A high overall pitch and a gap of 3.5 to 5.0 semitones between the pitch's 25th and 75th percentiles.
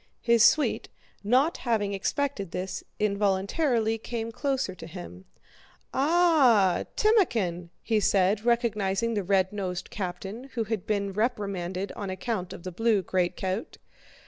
Yes: high, 205 Hz; average, 3.8 semitones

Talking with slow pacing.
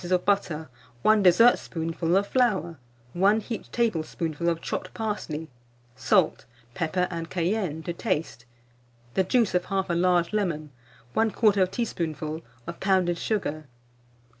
Yes: slow, 120 wpm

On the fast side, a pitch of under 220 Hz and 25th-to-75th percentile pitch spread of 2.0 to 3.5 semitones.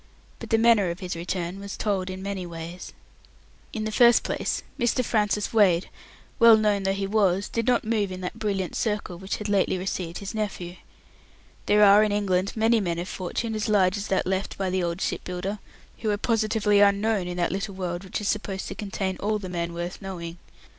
Yes: fast, 210 wpm; high, 195 Hz; average, 2.7 semitones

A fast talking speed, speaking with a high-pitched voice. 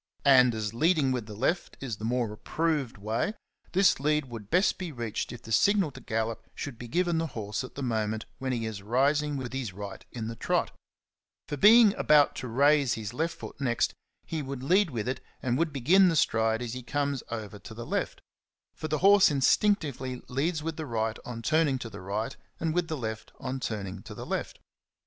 No: fast, 215 wpm; low, 130 Hz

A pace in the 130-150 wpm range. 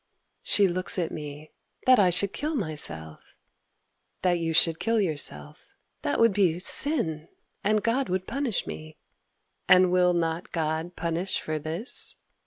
Yes: slow, 135 wpm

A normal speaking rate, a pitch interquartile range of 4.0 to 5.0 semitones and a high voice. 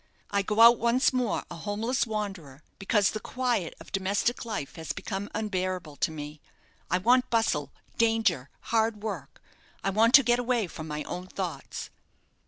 Yes: average, 165 wpm; average, 4.7 semitones; high, 205 Hz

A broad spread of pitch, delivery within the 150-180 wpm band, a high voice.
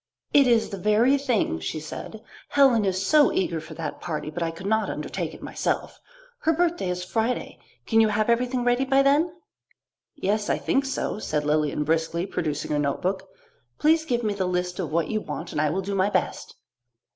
No: wide, 6.9 semitones; average, 200 wpm; high, 200 Hz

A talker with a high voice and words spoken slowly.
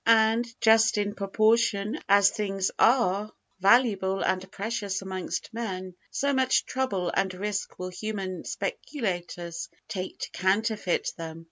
Yes: high, 200 Hz; slow, 125 wpm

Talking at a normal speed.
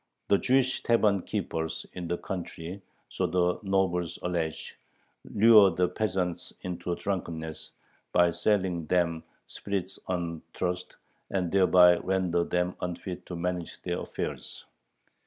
No: slow, 120 wpm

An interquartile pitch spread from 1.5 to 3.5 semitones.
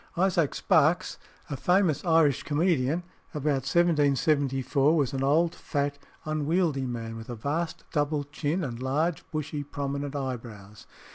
Yes: average, 3.1 semitones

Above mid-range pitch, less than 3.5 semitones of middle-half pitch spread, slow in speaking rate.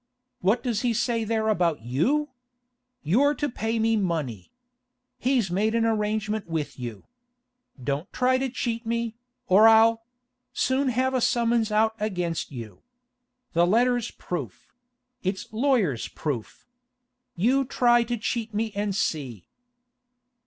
No: high, 220 Hz; average, 5.2 semitones; slow, 125 wpm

